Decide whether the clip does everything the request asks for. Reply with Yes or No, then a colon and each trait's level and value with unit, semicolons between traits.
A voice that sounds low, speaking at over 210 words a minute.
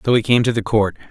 Yes: low, 110 Hz; fast, 325 wpm